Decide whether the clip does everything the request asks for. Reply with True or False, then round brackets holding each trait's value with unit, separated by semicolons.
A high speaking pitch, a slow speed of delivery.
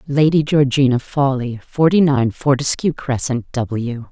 False (135 Hz; 115 wpm)